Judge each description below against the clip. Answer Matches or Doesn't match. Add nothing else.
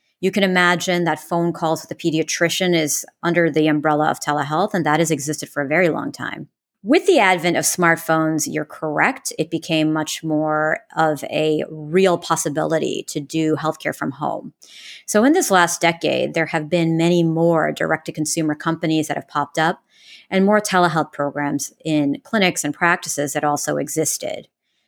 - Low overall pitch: Doesn't match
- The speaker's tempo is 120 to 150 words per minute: Doesn't match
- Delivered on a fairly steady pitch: Matches